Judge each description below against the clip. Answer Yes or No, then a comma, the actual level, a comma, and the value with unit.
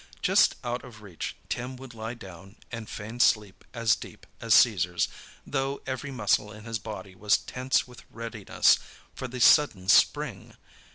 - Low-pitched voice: Yes, low, 115 Hz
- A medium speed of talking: Yes, average, 160 wpm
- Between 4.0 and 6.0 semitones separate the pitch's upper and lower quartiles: No, average, 3.3 semitones